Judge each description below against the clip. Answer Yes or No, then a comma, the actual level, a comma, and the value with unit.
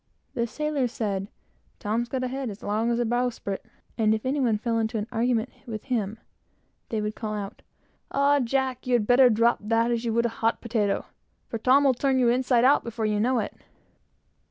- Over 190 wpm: Yes, fast, 205 wpm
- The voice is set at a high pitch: Yes, high, 235 Hz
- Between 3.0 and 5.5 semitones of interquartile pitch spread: No, narrow, 2.5 semitones